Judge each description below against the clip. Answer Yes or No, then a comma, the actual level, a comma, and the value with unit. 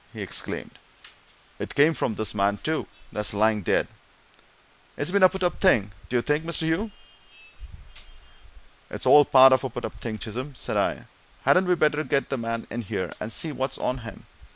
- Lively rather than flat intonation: Yes, wide, 6.1 semitones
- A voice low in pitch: Yes, low, 130 Hz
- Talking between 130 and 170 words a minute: No, average, 185 wpm